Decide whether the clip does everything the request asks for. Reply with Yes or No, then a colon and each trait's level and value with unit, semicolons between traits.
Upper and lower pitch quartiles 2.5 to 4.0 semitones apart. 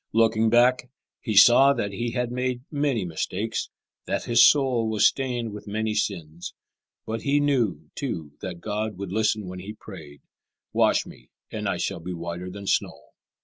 No: average, 4.8 semitones